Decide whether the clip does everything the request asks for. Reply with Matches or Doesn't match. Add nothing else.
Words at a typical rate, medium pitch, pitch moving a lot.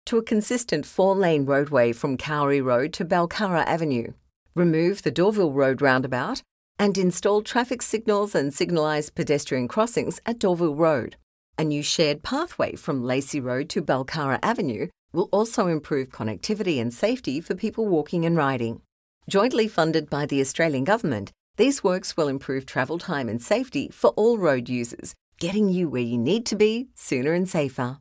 Matches